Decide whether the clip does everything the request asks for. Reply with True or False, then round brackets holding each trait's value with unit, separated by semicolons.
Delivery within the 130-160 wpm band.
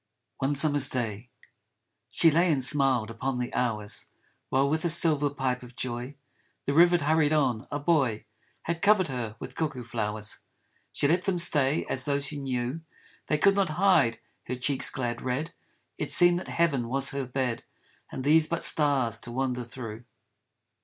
False (175 wpm)